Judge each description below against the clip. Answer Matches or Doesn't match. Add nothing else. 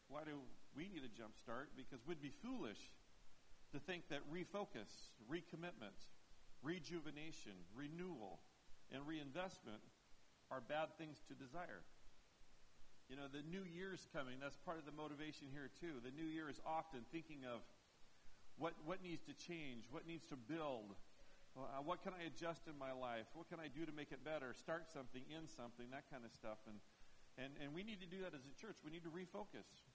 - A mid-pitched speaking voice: Matches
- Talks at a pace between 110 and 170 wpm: Doesn't match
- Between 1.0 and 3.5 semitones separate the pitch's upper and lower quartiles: Doesn't match